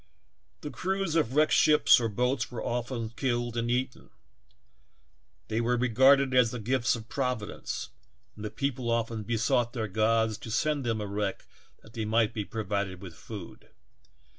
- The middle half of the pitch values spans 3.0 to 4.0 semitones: No, narrow, 2.5 semitones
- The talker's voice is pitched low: Yes, low, 115 Hz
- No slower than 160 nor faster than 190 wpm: Yes, average, 165 wpm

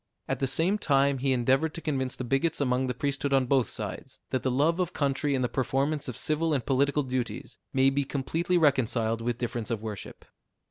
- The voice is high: No, low, 135 Hz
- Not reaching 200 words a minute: No, fast, 205 wpm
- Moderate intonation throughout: No, narrow, 2.3 semitones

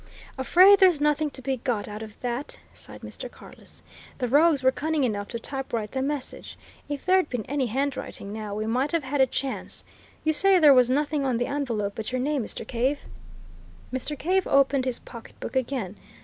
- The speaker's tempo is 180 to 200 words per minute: Yes, average, 190 wpm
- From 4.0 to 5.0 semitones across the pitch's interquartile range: No, average, 3.6 semitones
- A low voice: No, very high, 265 Hz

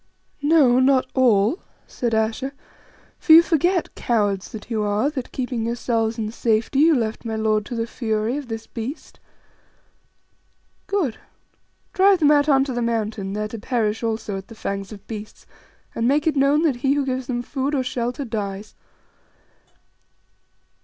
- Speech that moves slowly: No, average, 165 wpm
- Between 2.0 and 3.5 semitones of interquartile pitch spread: No, average, 4.1 semitones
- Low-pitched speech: No, high, 240 Hz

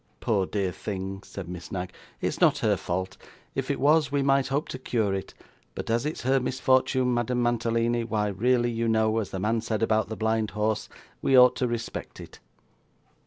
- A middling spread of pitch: Yes, average, 3.3 semitones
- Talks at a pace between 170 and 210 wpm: Yes, average, 195 wpm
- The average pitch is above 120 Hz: No, low, 115 Hz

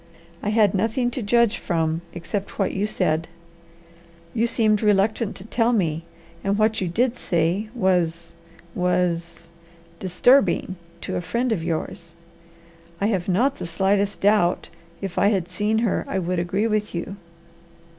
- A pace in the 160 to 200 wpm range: No, average, 150 wpm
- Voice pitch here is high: Yes, high, 195 Hz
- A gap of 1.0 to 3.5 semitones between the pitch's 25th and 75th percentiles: No, average, 3.9 semitones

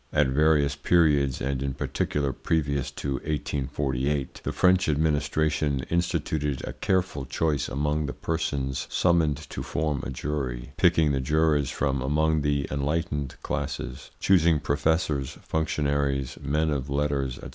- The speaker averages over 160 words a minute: No, slow, 135 wpm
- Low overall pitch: Yes, very low, 75 Hz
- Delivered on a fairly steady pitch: Yes, narrow, 2.2 semitones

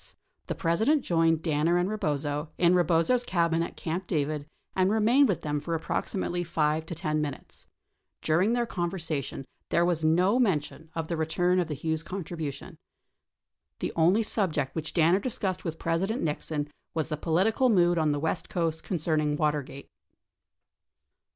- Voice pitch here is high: No, medium, 165 Hz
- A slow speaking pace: No, average, 160 wpm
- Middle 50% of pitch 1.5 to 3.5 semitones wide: Yes, average, 3.1 semitones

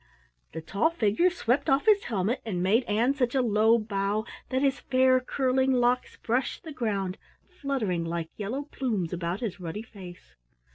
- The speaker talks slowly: No, average, 170 wpm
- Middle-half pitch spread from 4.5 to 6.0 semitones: Yes, average, 5.0 semitones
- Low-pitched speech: No, high, 230 Hz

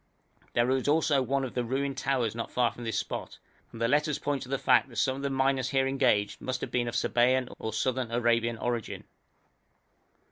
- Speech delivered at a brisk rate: Yes, fast, 210 wpm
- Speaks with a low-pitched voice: Yes, low, 130 Hz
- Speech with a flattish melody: Yes, narrow, 2.3 semitones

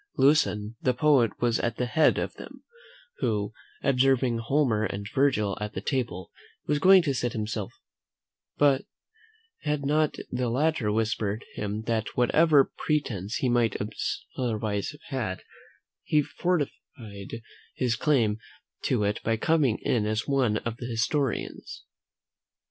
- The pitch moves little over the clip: No, average, 4.9 semitones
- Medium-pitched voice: No, low, 120 Hz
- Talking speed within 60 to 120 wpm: No, slow, 135 wpm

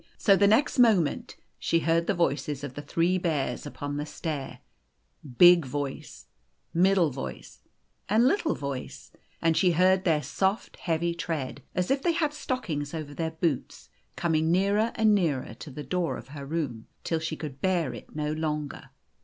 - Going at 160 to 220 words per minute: Yes, average, 170 wpm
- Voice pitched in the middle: Yes, medium, 165 Hz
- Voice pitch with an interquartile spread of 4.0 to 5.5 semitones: Yes, average, 4.4 semitones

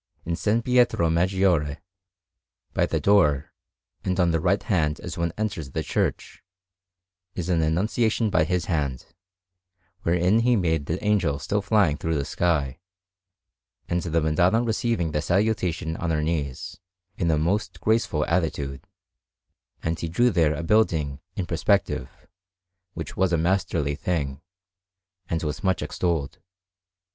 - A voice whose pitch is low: Yes, very low, 85 Hz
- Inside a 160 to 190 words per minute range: No, average, 140 wpm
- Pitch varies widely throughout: No, average, 3.8 semitones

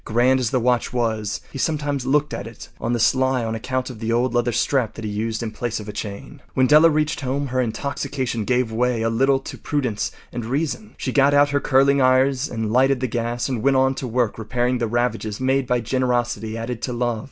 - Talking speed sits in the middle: No, fast, 225 wpm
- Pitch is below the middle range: Yes, low, 125 Hz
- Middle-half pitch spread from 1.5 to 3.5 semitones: Yes, average, 2.7 semitones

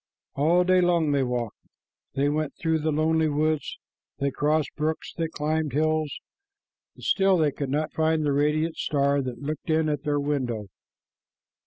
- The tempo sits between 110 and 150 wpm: No, average, 170 wpm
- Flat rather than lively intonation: Yes, narrow, 1.9 semitones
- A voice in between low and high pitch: Yes, medium, 150 Hz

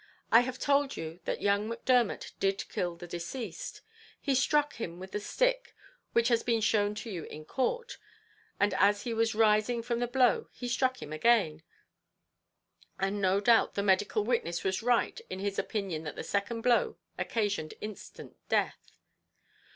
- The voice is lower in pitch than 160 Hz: No, high, 215 Hz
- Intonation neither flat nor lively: Yes, average, 3.9 semitones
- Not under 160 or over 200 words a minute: Yes, average, 165 wpm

